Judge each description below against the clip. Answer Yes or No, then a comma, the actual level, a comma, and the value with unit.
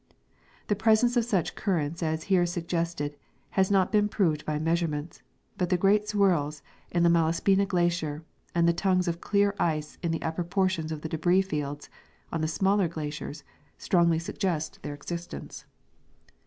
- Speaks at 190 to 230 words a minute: No, average, 160 wpm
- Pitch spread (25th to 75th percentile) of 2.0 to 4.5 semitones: Yes, average, 3.4 semitones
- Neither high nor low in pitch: Yes, medium, 170 Hz